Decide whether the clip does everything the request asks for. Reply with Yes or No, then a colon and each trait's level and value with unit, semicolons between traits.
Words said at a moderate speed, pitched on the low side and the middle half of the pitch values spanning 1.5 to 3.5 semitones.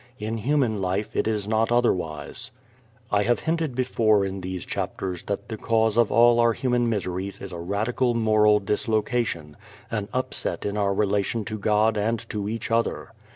Yes: average, 170 wpm; low, 110 Hz; average, 2.7 semitones